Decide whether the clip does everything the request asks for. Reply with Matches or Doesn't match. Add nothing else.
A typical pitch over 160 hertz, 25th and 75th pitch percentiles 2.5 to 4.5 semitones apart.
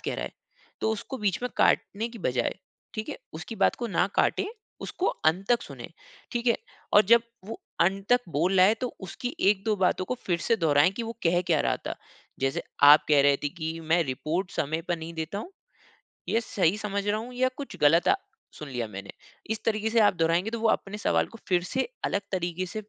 Doesn't match